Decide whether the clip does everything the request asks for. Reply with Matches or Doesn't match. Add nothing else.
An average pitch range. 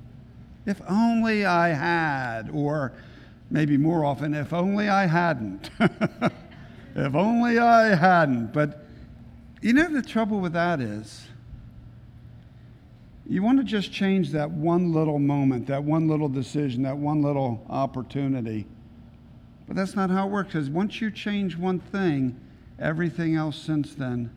Doesn't match